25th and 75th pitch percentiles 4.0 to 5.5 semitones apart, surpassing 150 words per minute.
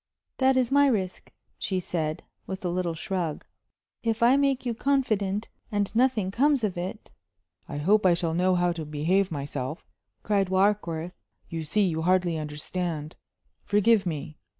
Yes: average, 4.7 semitones; average, 160 wpm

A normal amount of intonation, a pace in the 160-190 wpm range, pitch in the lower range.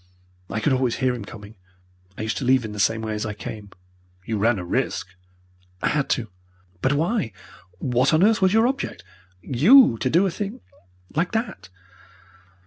No: wide, 8.4 semitones; average, 185 wpm; low, 130 Hz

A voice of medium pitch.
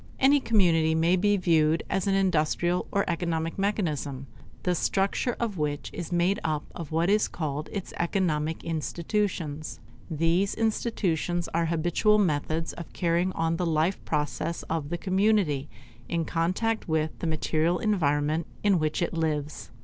Yes: medium, 170 Hz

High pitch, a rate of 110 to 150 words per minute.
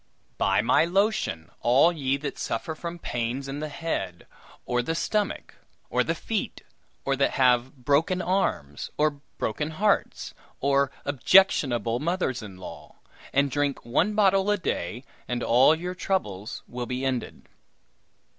No: medium, 140 Hz; average, 145 wpm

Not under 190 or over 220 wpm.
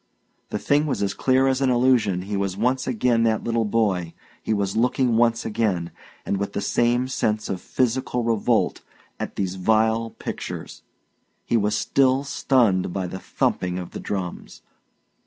No: average, 165 wpm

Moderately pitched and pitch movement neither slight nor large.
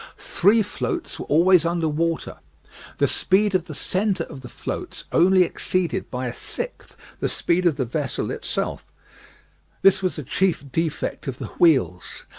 Yes: medium, 170 Hz; average, 4.1 semitones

